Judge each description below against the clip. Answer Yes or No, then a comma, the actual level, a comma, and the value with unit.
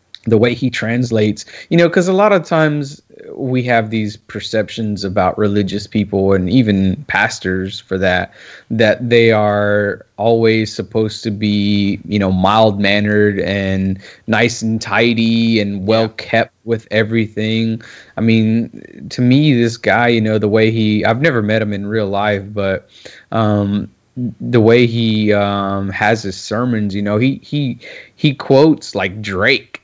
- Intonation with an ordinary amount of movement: No, narrow, 2.2 semitones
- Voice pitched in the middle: No, low, 110 Hz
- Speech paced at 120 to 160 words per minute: Yes, average, 155 wpm